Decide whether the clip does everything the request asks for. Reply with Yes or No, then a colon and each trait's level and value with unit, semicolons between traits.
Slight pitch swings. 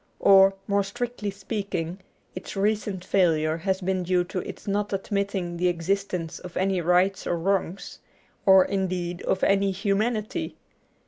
Yes: narrow, 1.9 semitones